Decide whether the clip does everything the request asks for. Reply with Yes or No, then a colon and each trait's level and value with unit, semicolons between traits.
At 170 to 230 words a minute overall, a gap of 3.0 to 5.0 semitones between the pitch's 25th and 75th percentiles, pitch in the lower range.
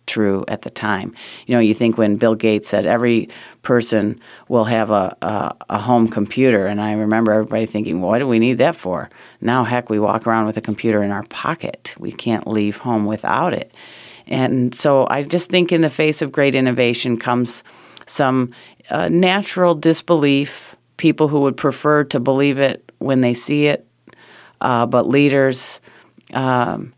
Yes: average, 180 wpm; average, 4.1 semitones; low, 125 Hz